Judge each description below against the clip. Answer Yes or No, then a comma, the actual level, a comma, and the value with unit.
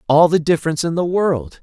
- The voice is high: No, medium, 160 Hz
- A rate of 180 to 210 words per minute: No, fast, 220 wpm